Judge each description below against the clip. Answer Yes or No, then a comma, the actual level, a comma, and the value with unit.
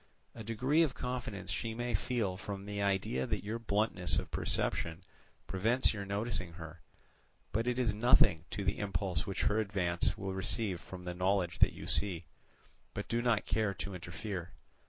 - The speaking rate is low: No, average, 175 wpm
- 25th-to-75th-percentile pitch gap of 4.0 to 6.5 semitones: No, average, 3.6 semitones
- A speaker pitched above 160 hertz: No, low, 100 Hz